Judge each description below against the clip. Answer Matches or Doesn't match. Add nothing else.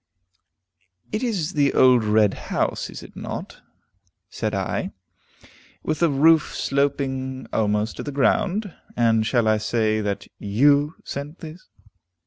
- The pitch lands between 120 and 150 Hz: Matches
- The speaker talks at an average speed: Doesn't match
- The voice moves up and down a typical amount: Doesn't match